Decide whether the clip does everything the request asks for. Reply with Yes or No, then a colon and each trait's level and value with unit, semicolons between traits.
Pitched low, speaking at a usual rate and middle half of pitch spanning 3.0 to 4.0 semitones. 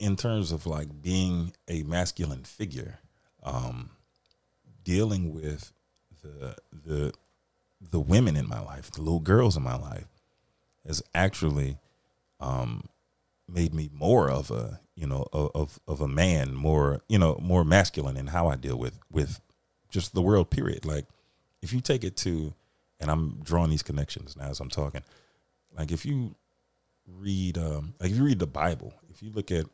No: very low, 80 Hz; average, 170 wpm; average, 4.6 semitones